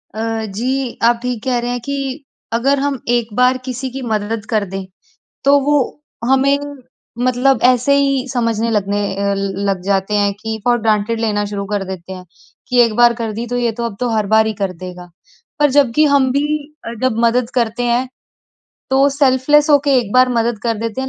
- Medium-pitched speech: No, high, 235 Hz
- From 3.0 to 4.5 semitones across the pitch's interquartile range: Yes, average, 3.6 semitones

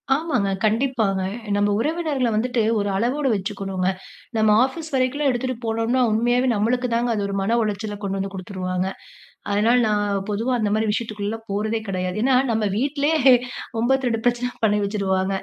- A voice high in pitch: Yes, high, 220 Hz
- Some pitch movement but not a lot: Yes, average, 3.8 semitones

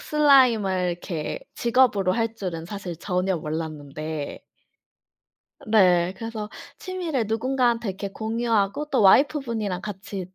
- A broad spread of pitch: No, average, 4.6 semitones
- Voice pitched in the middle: No, high, 205 Hz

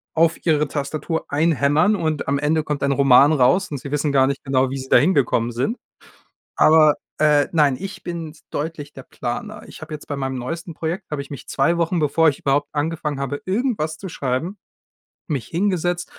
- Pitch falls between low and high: Yes, medium, 150 Hz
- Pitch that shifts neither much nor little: Yes, average, 3.1 semitones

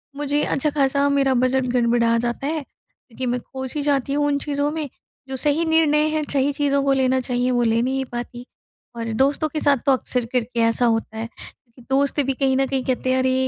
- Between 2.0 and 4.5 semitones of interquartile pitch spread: Yes, narrow, 2.5 semitones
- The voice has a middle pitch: No, very high, 265 Hz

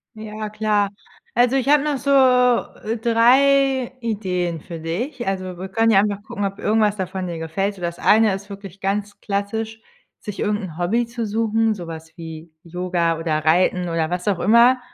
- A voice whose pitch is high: Yes, high, 205 Hz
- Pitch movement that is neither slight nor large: Yes, average, 4.2 semitones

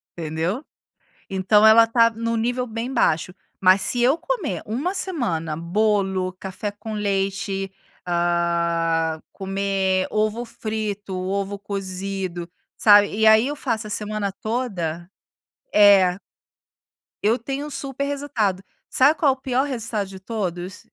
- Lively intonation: No, average, 3.6 semitones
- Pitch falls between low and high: No, high, 205 Hz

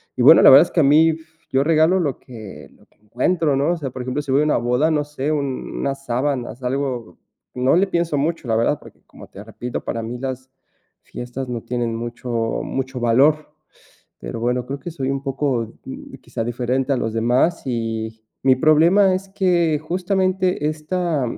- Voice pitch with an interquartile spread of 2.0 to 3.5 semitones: No, average, 4.3 semitones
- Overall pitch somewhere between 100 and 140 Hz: Yes, low, 135 Hz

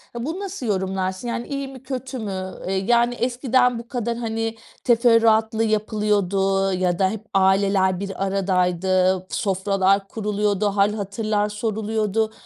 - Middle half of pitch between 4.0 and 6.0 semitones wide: No, average, 3.3 semitones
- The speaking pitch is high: Yes, high, 210 Hz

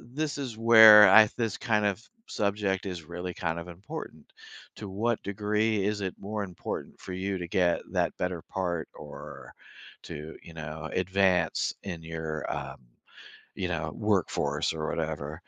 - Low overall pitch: Yes, very low, 95 Hz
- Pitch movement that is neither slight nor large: Yes, average, 4.0 semitones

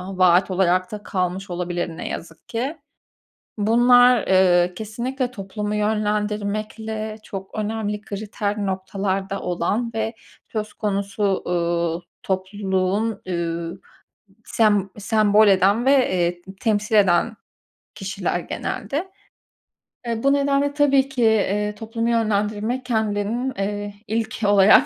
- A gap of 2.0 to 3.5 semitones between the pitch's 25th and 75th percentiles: Yes, average, 2.8 semitones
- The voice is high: Yes, high, 210 Hz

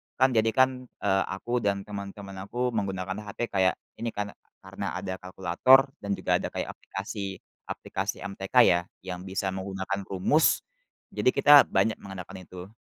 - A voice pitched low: Yes, low, 100 Hz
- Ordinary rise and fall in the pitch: Yes, average, 3.0 semitones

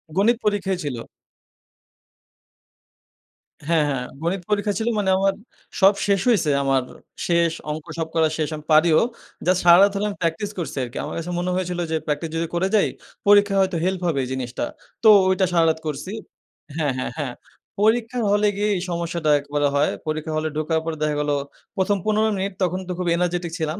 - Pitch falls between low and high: Yes, medium, 175 Hz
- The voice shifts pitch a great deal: No, average, 4.1 semitones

